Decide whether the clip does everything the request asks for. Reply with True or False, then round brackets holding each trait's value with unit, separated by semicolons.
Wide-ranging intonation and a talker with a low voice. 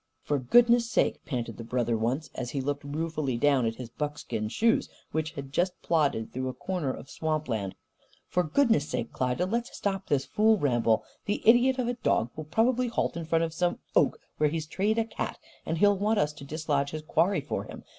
False (7.3 semitones; 155 Hz)